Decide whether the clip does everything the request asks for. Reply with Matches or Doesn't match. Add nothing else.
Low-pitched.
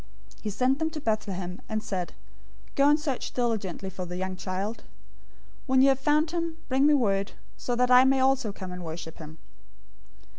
Doesn't match